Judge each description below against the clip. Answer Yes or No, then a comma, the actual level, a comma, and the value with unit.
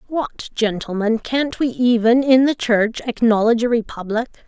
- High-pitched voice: Yes, high, 235 Hz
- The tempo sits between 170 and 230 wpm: No, average, 145 wpm